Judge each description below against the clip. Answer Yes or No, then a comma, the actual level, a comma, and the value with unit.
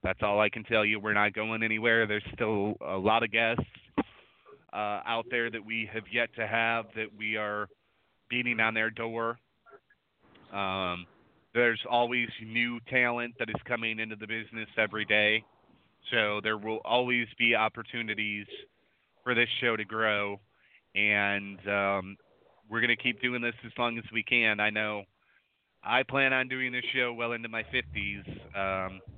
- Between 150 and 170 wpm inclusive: Yes, average, 165 wpm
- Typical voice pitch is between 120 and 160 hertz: No, low, 110 Hz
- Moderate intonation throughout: No, narrow, 2.0 semitones